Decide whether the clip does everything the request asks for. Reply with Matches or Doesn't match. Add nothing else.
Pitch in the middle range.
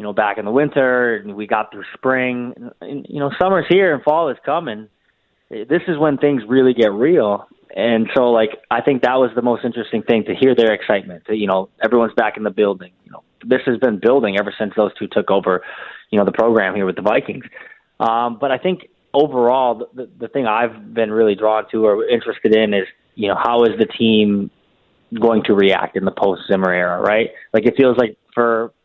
Doesn't match